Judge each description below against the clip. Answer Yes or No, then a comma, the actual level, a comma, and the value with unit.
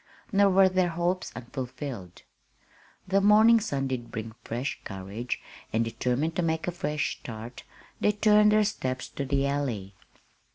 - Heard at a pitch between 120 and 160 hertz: Yes, medium, 140 Hz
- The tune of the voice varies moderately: No, wide, 7.8 semitones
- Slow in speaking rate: No, average, 150 wpm